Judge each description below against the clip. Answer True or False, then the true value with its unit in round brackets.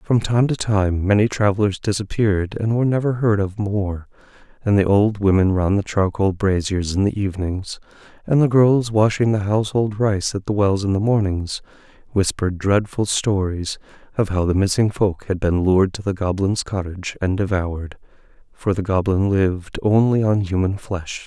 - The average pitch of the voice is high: False (100 Hz)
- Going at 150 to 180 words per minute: True (175 wpm)